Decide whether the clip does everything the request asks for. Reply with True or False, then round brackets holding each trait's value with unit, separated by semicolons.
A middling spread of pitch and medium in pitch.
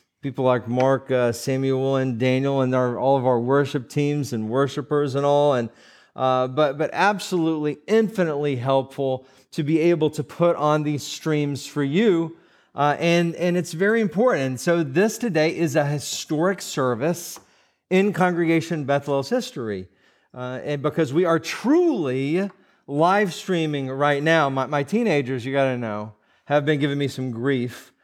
True (4.1 semitones; 145 Hz)